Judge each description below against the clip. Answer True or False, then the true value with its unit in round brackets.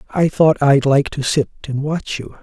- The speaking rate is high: True (225 wpm)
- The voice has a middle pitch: True (145 Hz)